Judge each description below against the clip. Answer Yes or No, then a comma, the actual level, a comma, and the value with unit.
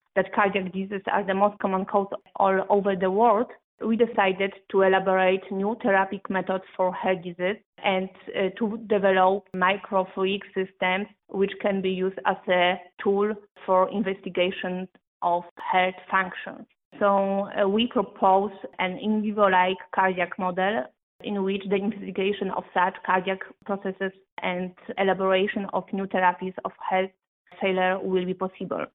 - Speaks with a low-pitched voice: No, high, 190 Hz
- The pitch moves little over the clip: Yes, narrow, 1.3 semitones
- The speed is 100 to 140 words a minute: Yes, slow, 135 wpm